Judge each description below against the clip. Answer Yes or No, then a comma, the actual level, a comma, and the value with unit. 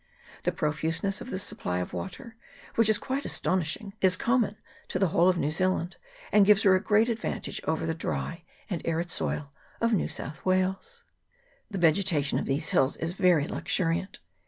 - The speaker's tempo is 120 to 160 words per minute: No, average, 180 wpm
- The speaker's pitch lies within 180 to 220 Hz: Yes, medium, 185 Hz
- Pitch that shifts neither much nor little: Yes, average, 4.0 semitones